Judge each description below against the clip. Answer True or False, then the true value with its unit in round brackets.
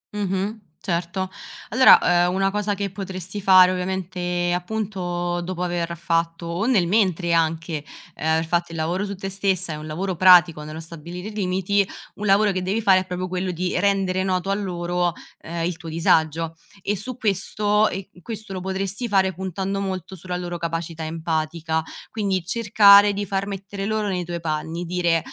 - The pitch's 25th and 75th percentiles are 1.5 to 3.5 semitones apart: True (2.6 semitones)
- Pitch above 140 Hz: True (185 Hz)